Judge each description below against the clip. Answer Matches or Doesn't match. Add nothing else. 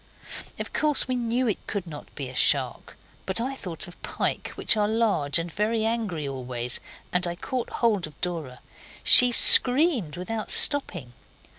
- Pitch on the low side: Doesn't match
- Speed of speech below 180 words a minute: Matches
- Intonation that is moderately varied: Doesn't match